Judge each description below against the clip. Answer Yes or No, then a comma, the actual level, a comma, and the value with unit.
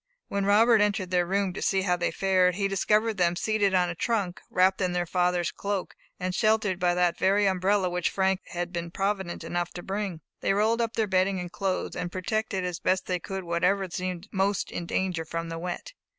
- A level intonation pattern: Yes, narrow, 2.0 semitones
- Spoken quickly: Yes, fast, 210 wpm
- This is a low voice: No, medium, 185 Hz